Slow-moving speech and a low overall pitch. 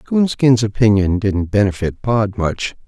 Yes: slow, 125 wpm; low, 110 Hz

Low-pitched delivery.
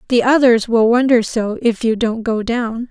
No: high, 235 Hz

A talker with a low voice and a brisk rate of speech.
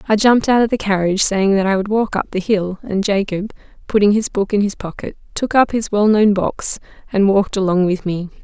No: high, 200 Hz; fast, 230 wpm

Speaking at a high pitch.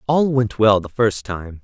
No: low, 115 Hz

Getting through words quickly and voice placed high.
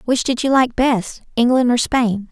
No: average, 180 wpm; high, 245 Hz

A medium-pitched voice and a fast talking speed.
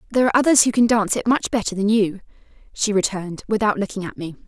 No: high, 210 Hz; fast, 230 wpm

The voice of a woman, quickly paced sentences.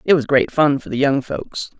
Yes: female; fast, 270 wpm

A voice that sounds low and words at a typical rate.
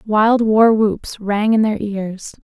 No: high, 215 Hz; average, 170 wpm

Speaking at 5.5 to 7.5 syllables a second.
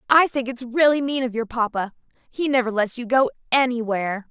Yes: 5.6 syllables/s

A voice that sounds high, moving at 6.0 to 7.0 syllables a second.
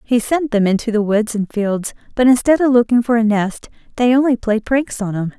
No: high, 230 Hz; 5.2 syllables/s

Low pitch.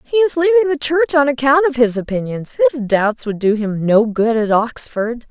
No: very high, 255 Hz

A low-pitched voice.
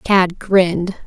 No: medium, 185 Hz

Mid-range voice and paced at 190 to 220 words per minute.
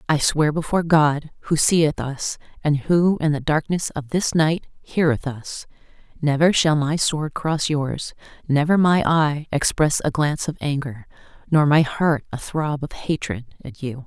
No: medium, 150 Hz; average, 170 wpm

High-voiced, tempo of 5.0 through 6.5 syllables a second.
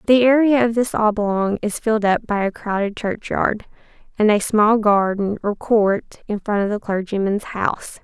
No: high, 210 Hz; 4.6 syllables/s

